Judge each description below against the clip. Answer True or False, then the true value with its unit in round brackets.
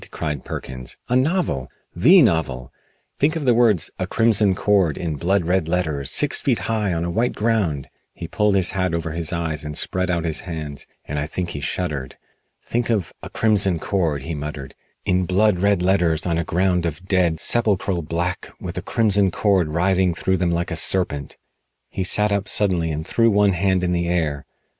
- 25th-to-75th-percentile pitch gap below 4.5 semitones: True (3.8 semitones)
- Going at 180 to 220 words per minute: True (195 wpm)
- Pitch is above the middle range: False (90 Hz)